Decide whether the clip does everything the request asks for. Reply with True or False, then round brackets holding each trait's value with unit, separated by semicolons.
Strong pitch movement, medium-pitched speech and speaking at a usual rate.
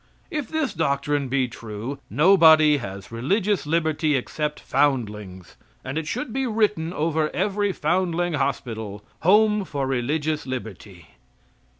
False (6.4 semitones; 150 Hz; 120 wpm)